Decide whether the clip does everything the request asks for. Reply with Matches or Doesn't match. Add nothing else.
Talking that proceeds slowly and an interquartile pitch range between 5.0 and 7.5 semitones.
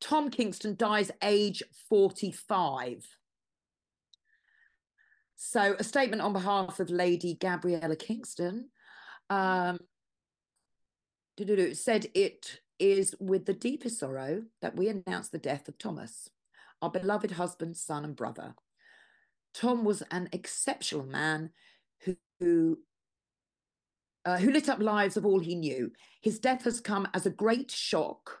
Matches